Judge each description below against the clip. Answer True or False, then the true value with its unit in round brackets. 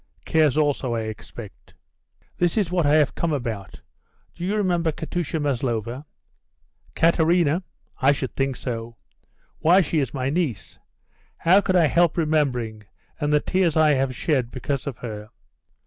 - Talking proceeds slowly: False (150 wpm)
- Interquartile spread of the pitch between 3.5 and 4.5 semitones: False (5.1 semitones)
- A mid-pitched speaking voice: True (145 Hz)